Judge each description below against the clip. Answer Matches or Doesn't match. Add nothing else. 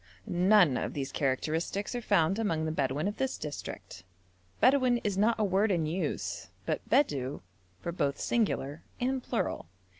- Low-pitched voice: Doesn't match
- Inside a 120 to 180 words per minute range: Matches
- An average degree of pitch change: Doesn't match